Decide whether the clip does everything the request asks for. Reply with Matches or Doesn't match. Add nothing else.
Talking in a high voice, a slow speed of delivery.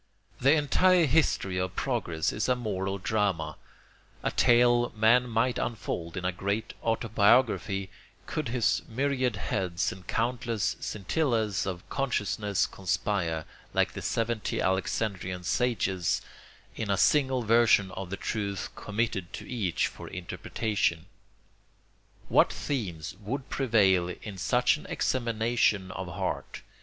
Doesn't match